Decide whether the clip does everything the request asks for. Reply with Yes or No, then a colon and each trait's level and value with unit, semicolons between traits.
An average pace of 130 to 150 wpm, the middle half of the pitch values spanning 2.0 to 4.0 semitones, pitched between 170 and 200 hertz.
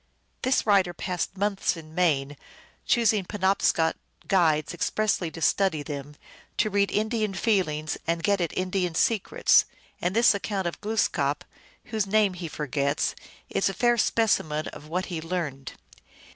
No: average, 145 wpm; average, 4.5 semitones; medium, 185 Hz